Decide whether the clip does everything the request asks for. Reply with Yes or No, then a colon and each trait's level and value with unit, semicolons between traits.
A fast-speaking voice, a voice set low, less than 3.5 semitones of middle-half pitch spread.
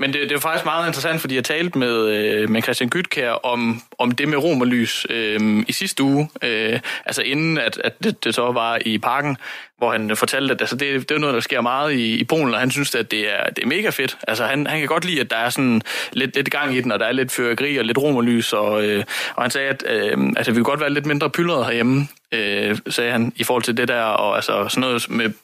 No: fast, 260 wpm; low, 125 Hz; average, 3.8 semitones